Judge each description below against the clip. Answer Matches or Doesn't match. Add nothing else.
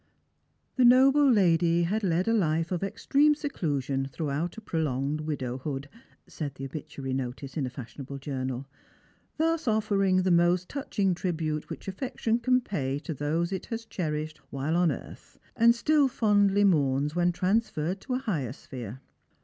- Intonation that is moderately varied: Doesn't match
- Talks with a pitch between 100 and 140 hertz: Doesn't match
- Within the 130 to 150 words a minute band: Doesn't match